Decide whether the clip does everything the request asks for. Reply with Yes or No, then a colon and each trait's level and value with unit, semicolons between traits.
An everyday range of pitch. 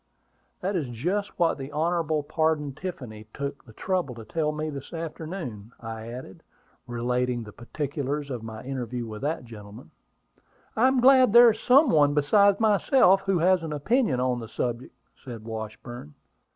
No: wide, 7.0 semitones